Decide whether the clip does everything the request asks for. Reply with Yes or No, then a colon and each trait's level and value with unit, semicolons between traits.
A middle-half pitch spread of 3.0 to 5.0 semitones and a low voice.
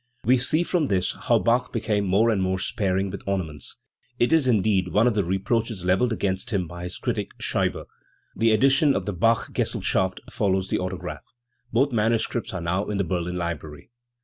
Yes: average, 3.9 semitones; low, 100 Hz